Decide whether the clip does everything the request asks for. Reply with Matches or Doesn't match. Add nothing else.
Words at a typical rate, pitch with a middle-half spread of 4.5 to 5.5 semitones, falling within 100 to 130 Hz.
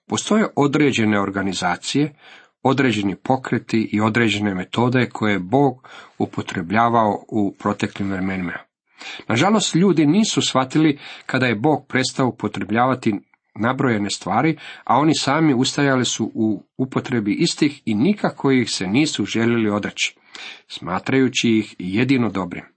Matches